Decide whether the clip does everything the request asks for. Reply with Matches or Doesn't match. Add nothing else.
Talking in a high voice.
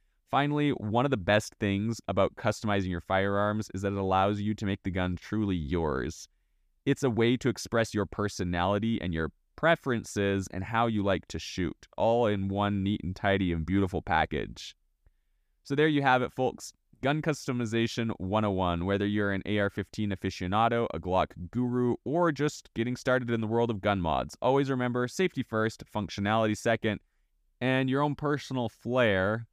Doesn't match